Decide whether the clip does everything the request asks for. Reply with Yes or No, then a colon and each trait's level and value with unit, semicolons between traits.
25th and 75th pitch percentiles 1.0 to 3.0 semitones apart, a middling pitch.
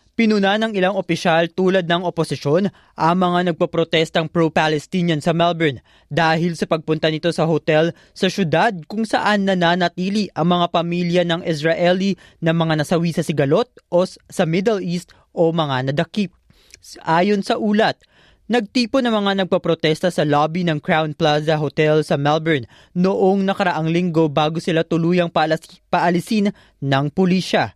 Yes: narrow, 2.6 semitones; medium, 170 Hz